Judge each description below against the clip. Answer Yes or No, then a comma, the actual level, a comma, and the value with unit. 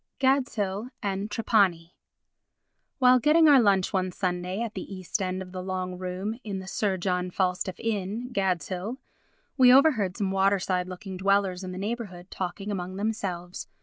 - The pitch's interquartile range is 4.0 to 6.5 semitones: No, average, 2.8 semitones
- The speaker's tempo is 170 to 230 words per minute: No, average, 155 wpm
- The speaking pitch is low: No, high, 190 Hz